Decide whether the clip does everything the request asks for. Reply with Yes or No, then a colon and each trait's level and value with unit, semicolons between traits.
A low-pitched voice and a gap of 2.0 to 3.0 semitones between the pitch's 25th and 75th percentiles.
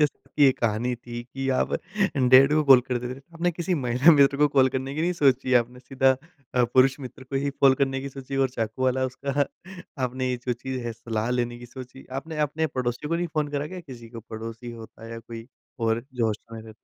Yes: low, 130 Hz; narrow, 2.5 semitones